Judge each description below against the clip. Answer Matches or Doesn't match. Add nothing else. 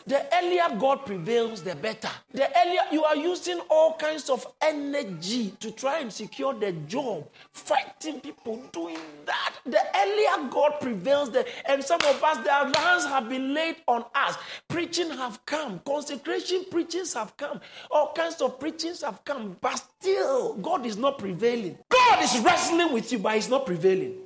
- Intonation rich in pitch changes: Matches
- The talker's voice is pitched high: Matches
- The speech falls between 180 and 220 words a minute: Doesn't match